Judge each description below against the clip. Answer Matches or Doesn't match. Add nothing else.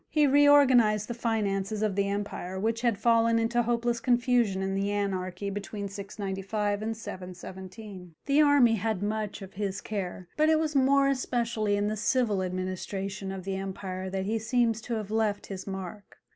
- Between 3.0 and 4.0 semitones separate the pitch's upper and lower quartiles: Matches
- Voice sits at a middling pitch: Doesn't match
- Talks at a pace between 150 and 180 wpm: Matches